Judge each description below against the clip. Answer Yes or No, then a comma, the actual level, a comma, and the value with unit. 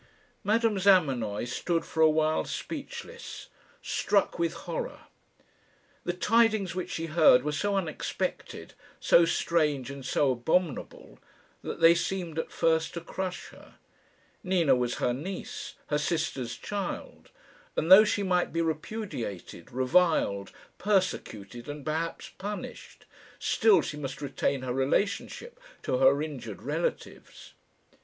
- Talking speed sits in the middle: No, slow, 125 wpm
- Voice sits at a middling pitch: Yes, medium, 160 Hz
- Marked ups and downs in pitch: Yes, wide, 5.9 semitones